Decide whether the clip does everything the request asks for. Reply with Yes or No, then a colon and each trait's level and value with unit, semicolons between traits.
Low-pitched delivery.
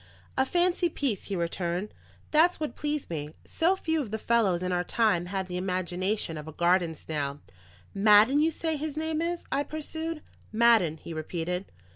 No: high, 210 Hz